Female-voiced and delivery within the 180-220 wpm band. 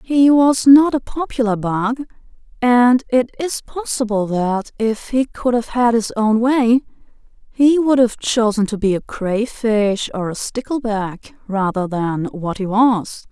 No: female; average, 160 wpm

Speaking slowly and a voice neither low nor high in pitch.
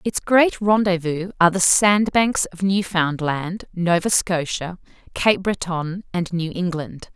Yes: slow, 125 wpm; medium, 180 Hz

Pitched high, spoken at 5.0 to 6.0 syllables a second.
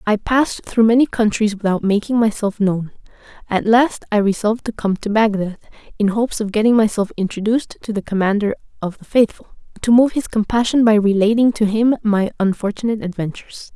Yes: high, 215 Hz; 5.8 syllables/s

